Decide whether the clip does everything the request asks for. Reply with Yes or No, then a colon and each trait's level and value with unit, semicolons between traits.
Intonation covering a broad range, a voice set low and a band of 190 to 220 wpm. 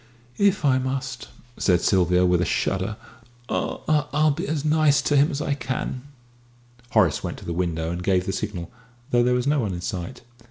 Yes: wide, 8.1 semitones; low, 125 Hz; average, 195 wpm